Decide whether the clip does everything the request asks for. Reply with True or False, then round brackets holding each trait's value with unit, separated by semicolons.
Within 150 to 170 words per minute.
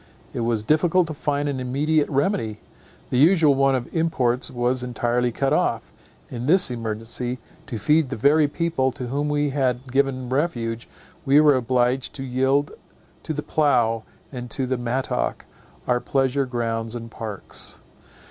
True (155 wpm)